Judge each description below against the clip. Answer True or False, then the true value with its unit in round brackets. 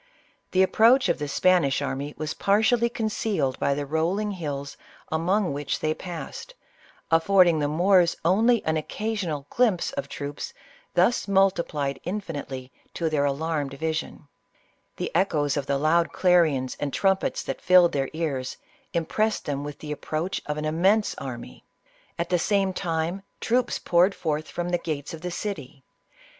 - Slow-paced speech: False (155 wpm)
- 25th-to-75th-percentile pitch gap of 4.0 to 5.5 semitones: True (4.7 semitones)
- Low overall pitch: False (165 Hz)